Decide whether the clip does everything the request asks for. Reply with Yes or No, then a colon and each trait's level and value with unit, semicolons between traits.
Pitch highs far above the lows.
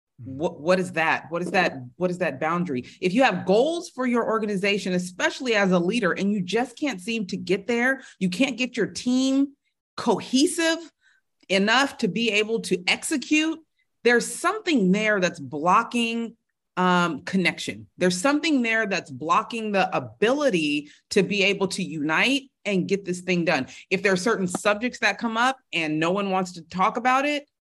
Yes: wide, 6.0 semitones